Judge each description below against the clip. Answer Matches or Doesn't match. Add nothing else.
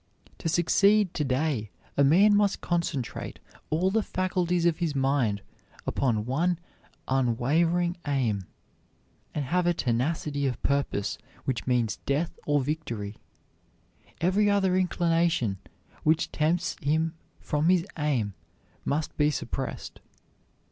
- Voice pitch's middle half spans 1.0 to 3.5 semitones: Doesn't match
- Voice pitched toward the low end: Doesn't match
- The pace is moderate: Doesn't match